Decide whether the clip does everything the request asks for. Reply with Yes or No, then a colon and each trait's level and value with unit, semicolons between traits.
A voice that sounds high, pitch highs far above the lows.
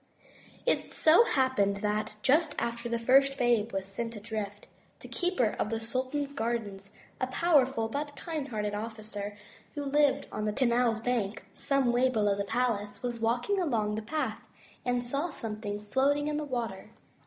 No: high, 235 Hz; average, 4.4 semitones